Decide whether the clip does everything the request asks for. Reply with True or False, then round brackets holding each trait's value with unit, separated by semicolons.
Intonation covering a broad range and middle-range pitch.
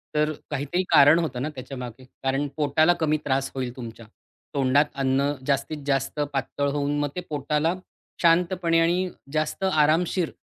False (2.8 semitones; 145 Hz)